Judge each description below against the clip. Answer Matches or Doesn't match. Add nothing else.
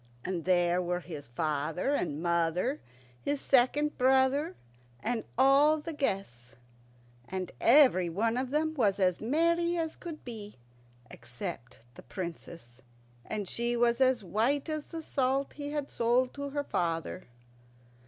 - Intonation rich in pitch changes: Matches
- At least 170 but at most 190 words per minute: Doesn't match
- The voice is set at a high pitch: Matches